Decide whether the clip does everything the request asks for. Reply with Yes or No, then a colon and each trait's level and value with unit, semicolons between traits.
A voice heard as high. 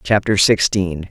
No: very low, 95 Hz